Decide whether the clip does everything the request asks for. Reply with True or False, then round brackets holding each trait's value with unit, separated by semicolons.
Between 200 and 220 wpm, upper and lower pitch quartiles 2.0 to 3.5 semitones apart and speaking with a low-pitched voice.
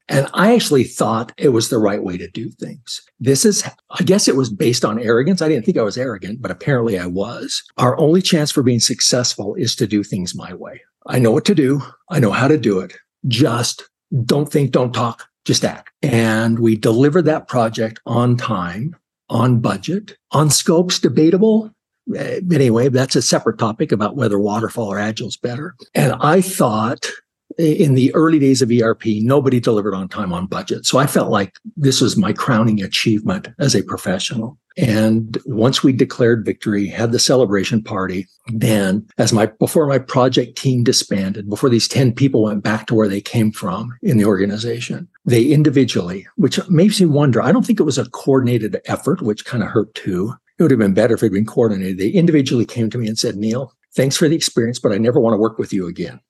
False (205 wpm; 5.3 semitones; 125 Hz)